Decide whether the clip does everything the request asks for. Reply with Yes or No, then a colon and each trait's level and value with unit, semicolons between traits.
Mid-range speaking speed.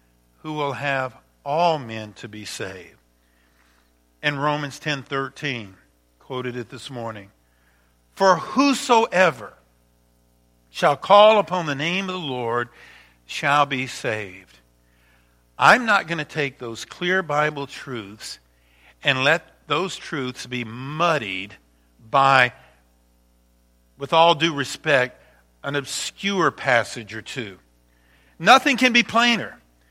No: slow, 115 wpm